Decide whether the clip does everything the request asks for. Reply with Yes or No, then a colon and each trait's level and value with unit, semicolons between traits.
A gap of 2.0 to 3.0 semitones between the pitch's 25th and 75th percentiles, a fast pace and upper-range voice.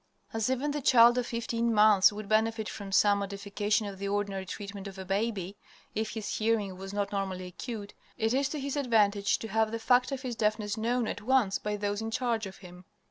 Yes: narrow, 2.6 semitones; fast, 215 wpm; high, 215 Hz